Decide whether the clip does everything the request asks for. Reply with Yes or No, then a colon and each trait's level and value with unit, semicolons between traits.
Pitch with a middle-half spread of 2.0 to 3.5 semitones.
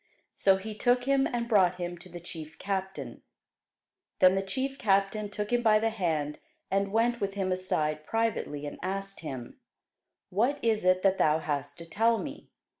No: average, 4.2 semitones